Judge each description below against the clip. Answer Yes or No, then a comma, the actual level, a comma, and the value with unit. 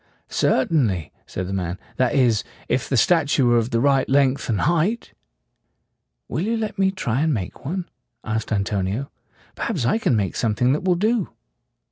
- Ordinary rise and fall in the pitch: No, wide, 7.7 semitones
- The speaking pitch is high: No, low, 130 Hz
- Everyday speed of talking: Yes, average, 185 wpm